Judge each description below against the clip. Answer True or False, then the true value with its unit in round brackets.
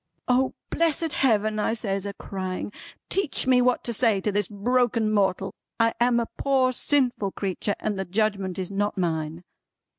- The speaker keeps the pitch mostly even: False (4.2 semitones)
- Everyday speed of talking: True (170 wpm)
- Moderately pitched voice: False (215 Hz)